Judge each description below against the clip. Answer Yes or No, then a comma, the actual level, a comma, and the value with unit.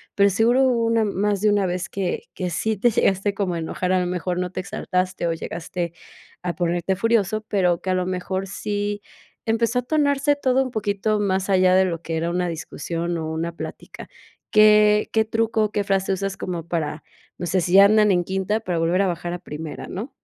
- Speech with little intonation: No, average, 3.2 semitones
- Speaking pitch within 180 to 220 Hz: Yes, high, 190 Hz